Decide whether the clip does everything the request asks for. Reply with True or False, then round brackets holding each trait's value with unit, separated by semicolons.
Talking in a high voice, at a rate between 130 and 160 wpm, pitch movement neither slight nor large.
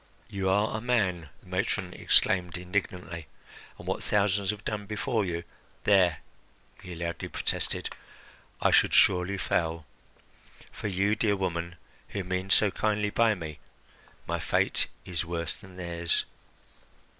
False (95 Hz; 140 wpm; 3.0 semitones)